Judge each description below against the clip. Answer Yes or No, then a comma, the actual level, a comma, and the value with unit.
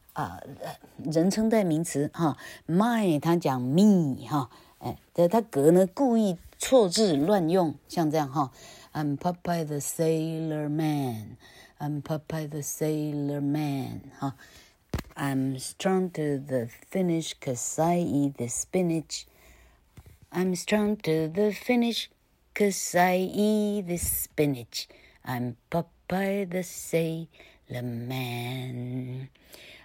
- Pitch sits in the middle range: Yes, medium, 155 Hz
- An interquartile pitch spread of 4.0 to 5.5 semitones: Yes, average, 5.1 semitones